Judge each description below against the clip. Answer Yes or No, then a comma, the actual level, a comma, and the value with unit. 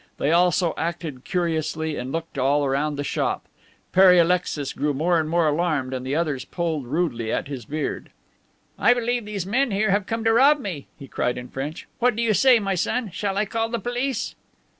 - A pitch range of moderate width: No, wide, 6.4 semitones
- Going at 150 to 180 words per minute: No, fast, 205 wpm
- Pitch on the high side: No, medium, 170 Hz